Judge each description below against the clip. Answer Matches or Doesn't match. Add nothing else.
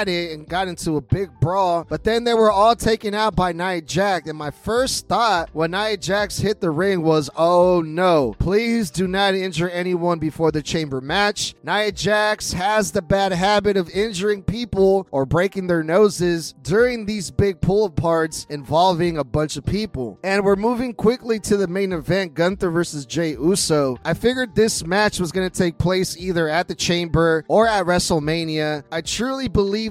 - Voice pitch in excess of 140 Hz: Matches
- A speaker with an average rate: Matches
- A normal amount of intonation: Matches